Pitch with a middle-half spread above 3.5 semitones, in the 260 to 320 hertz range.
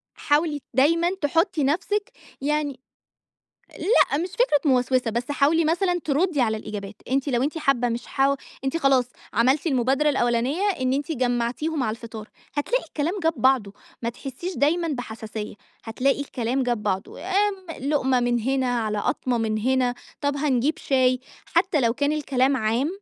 Yes: average, 4.1 semitones; very high, 270 Hz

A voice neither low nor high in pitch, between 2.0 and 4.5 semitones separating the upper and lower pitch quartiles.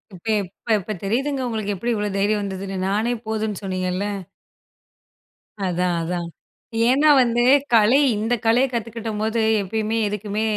No: high, 215 Hz; average, 2.8 semitones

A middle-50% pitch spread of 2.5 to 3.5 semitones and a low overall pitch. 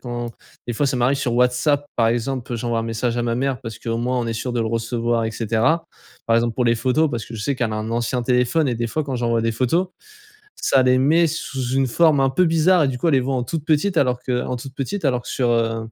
Yes: average, 2.8 semitones; low, 125 Hz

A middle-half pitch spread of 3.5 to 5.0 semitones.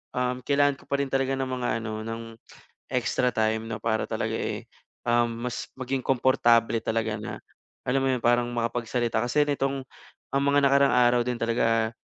No: narrow, 2.5 semitones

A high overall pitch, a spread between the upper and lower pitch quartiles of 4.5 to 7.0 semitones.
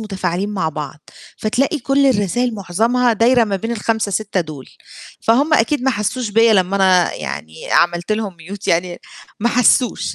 Yes: high, 210 Hz; average, 4.8 semitones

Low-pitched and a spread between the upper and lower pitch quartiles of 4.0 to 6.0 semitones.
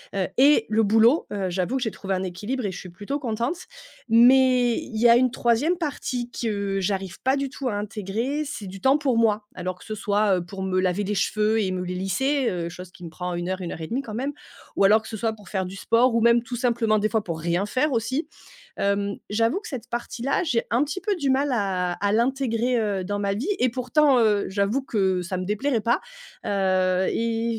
No: high, 220 Hz; average, 4.6 semitones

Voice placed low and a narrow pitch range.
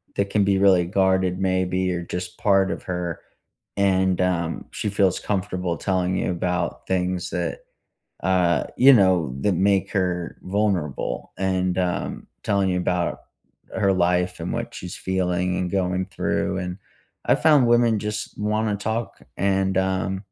Yes: very low, 95 Hz; narrow, 1.6 semitones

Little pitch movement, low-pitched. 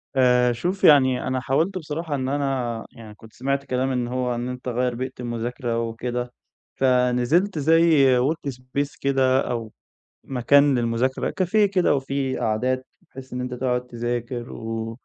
Yes: narrow, 2.2 semitones; low, 130 Hz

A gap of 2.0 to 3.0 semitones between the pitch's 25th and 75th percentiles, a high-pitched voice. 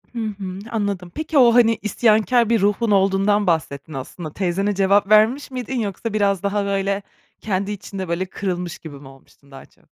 Yes: average, 2.7 semitones; high, 200 Hz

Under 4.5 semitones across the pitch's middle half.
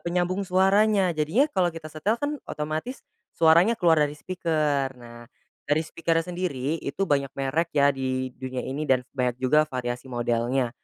No: average, 5.2 semitones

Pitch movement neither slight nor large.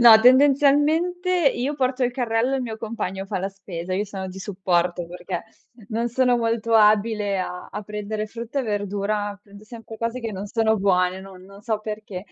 Yes: average, 3.3 semitones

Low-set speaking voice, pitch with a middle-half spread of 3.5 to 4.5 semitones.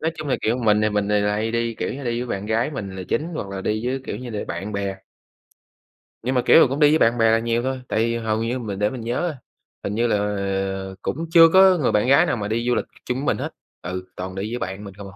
Yes: low, 115 Hz; average, 3.8 semitones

